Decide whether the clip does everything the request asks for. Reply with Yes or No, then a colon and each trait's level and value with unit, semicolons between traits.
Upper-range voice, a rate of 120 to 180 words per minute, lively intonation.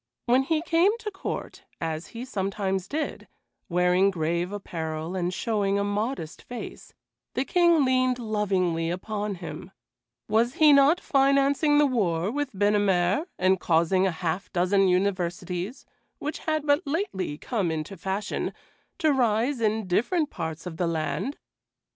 Yes: high, 205 Hz; average, 140 wpm; wide, 7.3 semitones